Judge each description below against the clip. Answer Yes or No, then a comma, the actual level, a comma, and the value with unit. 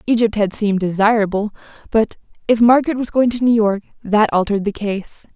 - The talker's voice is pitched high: Yes, high, 215 Hz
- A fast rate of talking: No, average, 180 wpm